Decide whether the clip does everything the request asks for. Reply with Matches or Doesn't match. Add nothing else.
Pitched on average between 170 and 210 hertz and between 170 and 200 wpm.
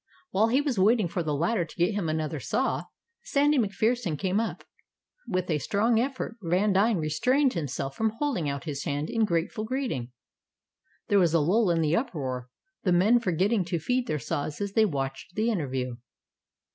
Matches